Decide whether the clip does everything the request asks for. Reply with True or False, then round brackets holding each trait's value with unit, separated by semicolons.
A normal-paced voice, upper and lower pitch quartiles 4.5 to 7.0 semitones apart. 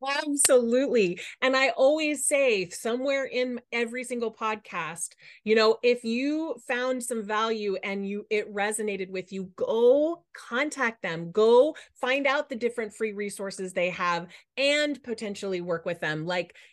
True (145 wpm; 4.8 semitones)